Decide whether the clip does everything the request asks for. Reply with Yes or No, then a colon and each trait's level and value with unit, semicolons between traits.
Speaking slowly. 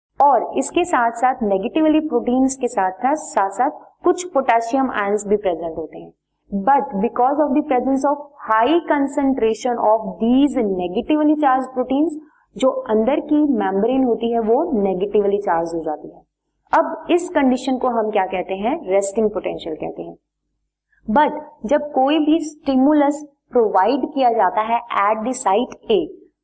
No: average, 145 wpm